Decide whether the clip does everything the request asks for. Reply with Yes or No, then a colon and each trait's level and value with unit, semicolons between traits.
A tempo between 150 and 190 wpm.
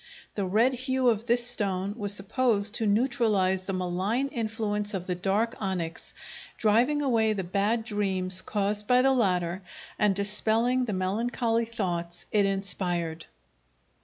No: average, 140 wpm